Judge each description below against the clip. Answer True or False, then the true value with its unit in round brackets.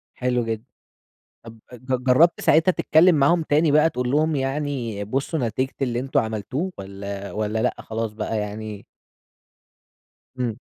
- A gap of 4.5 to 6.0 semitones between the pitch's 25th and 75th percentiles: True (5.0 semitones)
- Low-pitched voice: True (125 Hz)